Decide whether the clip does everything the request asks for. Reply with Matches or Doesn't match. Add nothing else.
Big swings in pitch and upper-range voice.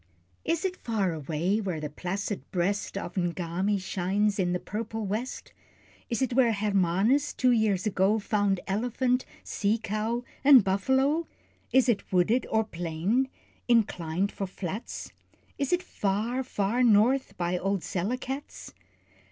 Doesn't match